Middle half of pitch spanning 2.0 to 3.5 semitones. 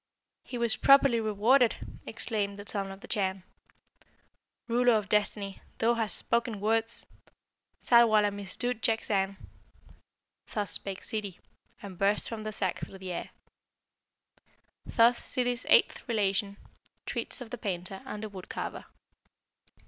Yes: average, 2.9 semitones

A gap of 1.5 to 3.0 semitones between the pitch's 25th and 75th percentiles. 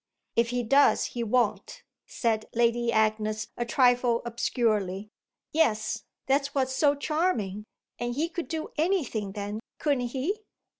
No: average, 4.6 semitones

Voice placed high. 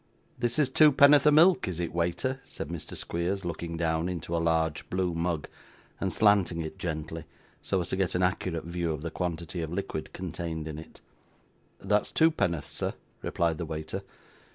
No: very low, 85 Hz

